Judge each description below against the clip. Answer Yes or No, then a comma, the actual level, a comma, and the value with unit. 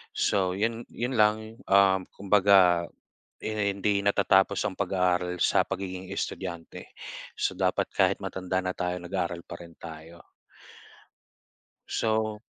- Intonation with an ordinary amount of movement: No, narrow, 2.2 semitones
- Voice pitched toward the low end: Yes, very low, 95 Hz